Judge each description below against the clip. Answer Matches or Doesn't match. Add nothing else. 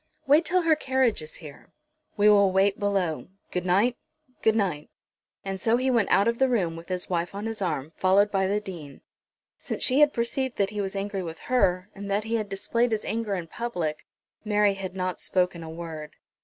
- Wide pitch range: Doesn't match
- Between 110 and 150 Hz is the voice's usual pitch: Doesn't match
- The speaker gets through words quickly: Matches